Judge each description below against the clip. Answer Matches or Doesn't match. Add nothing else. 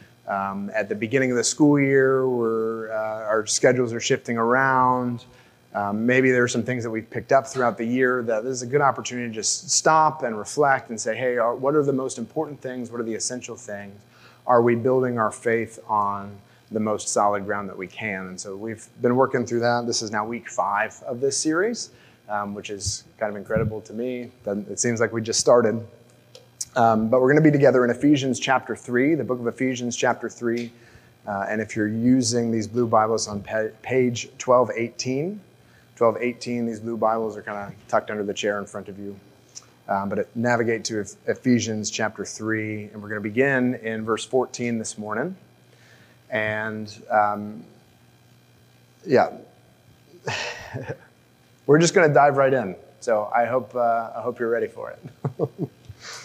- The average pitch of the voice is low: Matches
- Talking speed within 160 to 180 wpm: Doesn't match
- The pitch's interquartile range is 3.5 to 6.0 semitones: Doesn't match